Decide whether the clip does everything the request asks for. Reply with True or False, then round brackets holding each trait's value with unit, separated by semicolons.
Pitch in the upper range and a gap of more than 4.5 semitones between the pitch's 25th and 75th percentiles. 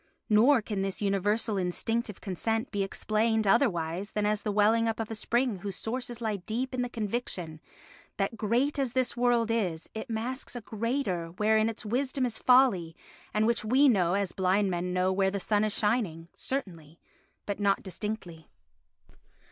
False (215 Hz; 3.4 semitones)